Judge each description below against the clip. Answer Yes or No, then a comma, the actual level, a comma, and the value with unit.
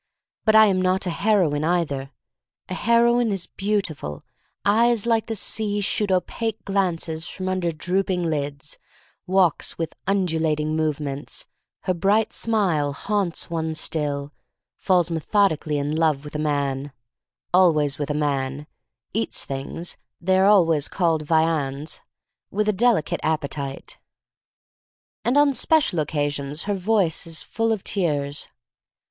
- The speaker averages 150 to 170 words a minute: No, average, 140 wpm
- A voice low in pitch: No, medium, 170 Hz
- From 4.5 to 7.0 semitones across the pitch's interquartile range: Yes, average, 5.1 semitones